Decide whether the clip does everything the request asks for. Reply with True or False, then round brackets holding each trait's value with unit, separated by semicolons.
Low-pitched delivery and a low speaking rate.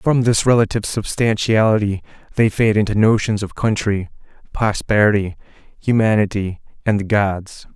True (105 Hz; 115 wpm)